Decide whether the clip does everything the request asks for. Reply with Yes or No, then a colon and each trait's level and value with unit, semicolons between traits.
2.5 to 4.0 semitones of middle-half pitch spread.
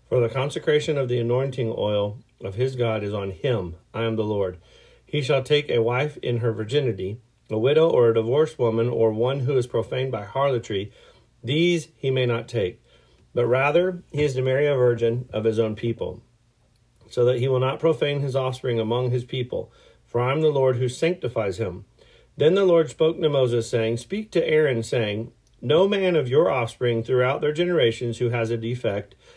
Yes: average, 3.6 semitones